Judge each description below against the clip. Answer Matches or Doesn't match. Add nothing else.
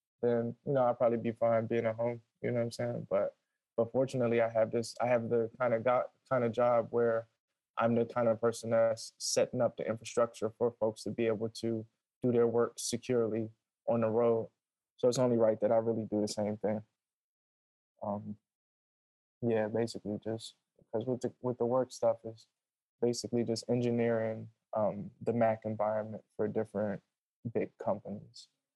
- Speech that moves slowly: Doesn't match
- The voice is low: Matches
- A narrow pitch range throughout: Matches